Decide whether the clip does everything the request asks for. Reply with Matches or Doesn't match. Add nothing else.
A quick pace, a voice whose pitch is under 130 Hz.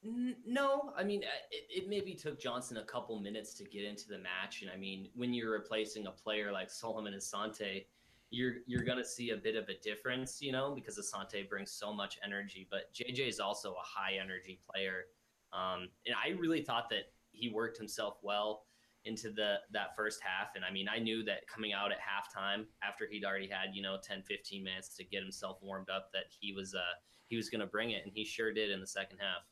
Matches